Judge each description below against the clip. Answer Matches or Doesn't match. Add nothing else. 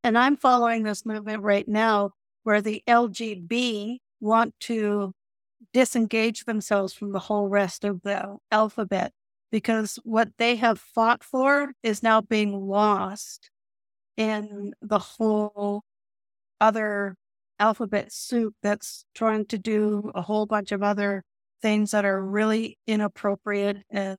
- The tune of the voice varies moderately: Doesn't match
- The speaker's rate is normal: Doesn't match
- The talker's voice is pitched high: Matches